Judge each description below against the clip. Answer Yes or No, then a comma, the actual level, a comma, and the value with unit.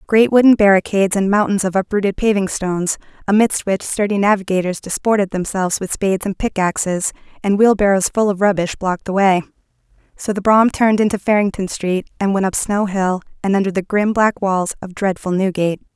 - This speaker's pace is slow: No, average, 180 wpm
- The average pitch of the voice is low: No, high, 195 Hz